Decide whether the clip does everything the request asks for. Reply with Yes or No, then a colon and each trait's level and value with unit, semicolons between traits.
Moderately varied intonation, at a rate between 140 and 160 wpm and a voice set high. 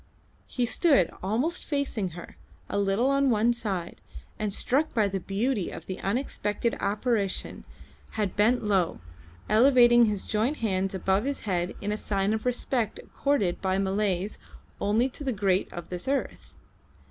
Yes: average, 4.1 semitones; average, 155 wpm; high, 210 Hz